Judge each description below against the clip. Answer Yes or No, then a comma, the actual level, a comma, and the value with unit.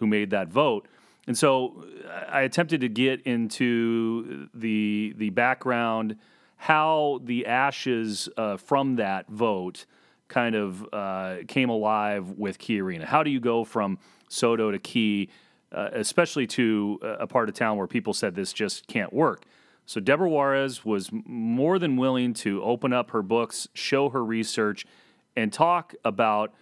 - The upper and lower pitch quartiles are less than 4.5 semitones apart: Yes, average, 3.8 semitones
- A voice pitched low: Yes, low, 115 Hz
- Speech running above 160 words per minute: No, average, 155 wpm